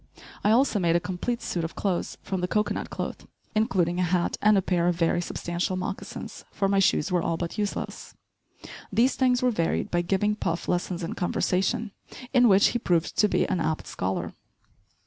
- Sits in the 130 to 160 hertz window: No, medium, 185 Hz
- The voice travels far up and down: No, average, 3.4 semitones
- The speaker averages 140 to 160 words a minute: No, average, 190 wpm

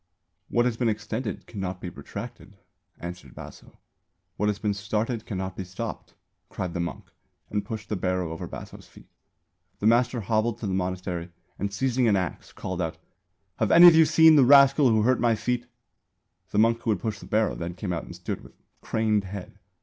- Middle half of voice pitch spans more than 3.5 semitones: Yes, average, 4.2 semitones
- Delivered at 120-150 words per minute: No, average, 195 wpm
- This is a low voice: Yes, low, 105 Hz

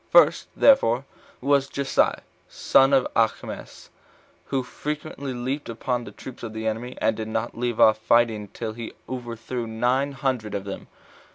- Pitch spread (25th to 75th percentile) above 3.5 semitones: No, average, 3.2 semitones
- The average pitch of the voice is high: No, low, 120 Hz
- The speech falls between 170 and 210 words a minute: No, average, 160 wpm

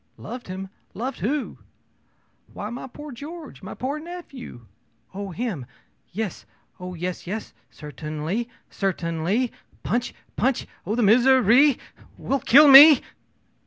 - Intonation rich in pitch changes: Yes, wide, 6.5 semitones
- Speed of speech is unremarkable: No, slow, 120 wpm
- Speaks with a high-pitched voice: Yes, high, 235 Hz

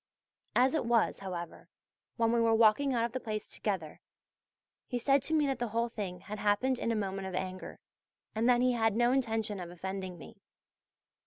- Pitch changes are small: No, average, 3.8 semitones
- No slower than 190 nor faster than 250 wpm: Yes, average, 195 wpm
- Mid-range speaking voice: No, high, 225 Hz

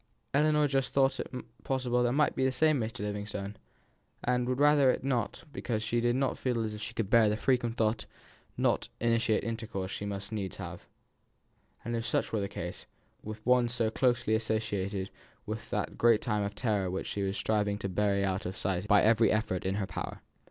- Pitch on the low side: Yes, low, 110 Hz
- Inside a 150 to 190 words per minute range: No, average, 200 wpm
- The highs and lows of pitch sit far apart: No, average, 3.3 semitones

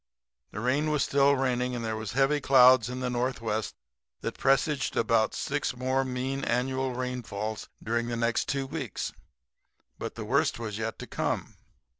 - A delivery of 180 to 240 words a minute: No, average, 165 wpm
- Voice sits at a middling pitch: No, low, 125 Hz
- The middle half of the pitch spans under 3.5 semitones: Yes, narrow, 2.5 semitones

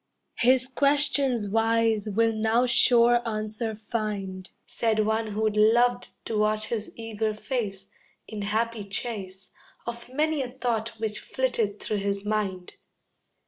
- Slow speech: Yes, slow, 130 wpm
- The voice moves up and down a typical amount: No, narrow, 2.1 semitones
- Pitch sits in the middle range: No, high, 220 Hz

